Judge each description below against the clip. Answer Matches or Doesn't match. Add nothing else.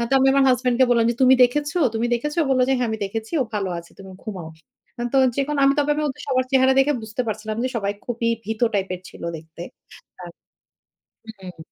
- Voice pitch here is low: Doesn't match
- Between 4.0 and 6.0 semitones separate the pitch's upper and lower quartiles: Matches